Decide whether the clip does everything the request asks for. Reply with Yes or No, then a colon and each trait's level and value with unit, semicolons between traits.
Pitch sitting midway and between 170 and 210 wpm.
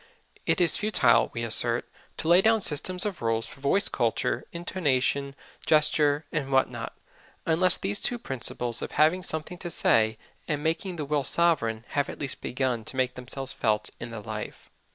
Yes: medium, 145 Hz; average, 175 wpm